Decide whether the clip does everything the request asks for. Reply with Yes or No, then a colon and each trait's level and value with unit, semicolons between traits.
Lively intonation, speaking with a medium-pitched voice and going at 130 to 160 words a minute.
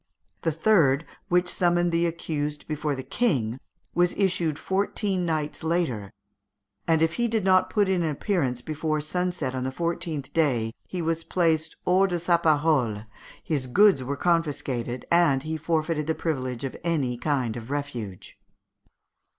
No: average, 4.3 semitones; medium, 160 Hz; average, 155 wpm